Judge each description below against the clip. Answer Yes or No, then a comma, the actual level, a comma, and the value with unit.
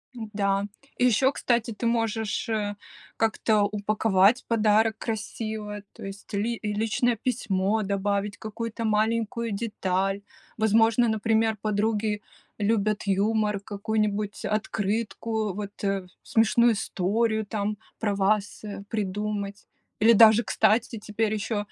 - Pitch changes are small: Yes, narrow, 1.7 semitones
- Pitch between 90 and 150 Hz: No, high, 215 Hz